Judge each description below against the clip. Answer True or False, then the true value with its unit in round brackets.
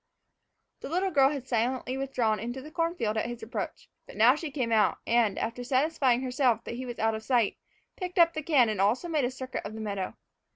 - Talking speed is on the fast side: True (225 wpm)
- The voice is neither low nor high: False (250 Hz)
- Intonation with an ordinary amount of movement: True (4.1 semitones)